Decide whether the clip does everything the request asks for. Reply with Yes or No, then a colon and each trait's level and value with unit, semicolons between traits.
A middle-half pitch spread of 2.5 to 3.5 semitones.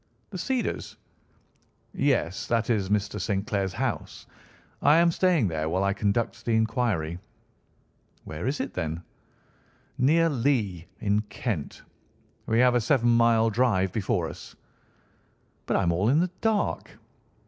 No: average, 5.0 semitones